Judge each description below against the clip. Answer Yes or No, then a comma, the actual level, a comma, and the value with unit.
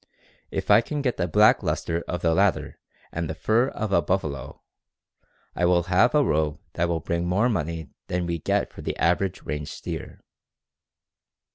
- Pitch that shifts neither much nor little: Yes, average, 3.6 semitones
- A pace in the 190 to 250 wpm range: No, average, 175 wpm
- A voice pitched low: Yes, very low, 85 Hz